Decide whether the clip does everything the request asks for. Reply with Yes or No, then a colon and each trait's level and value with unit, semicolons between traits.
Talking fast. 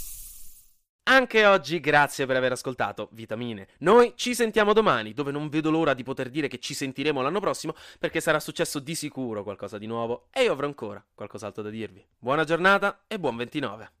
Yes: fast, 185 wpm